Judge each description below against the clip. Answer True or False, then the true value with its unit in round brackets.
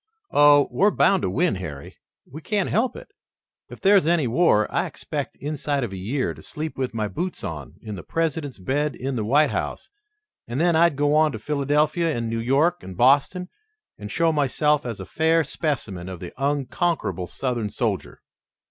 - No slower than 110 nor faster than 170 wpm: False (185 wpm)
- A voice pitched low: False (145 Hz)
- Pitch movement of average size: False (6.1 semitones)